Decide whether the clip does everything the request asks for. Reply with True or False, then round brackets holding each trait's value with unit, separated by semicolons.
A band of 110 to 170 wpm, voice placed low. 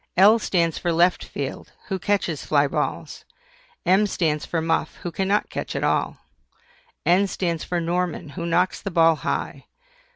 False (160 wpm; 175 Hz)